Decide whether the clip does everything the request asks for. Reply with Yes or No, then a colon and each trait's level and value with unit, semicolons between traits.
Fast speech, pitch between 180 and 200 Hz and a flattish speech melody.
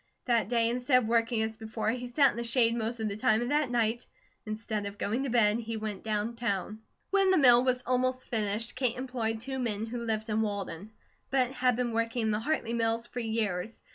No: fast, 225 wpm; high, 230 Hz; narrow, 2.1 semitones